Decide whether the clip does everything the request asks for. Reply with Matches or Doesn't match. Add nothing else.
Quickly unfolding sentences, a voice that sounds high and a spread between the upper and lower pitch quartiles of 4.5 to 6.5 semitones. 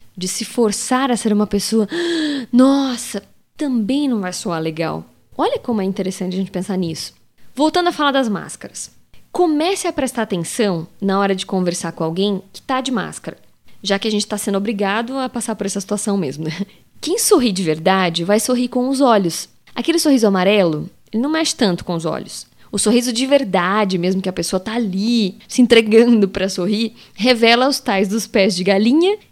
Matches